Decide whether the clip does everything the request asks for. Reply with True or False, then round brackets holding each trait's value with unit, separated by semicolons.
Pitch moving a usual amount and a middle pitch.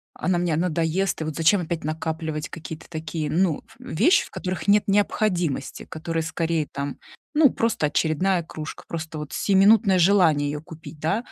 True (3.2 semitones; 165 Hz)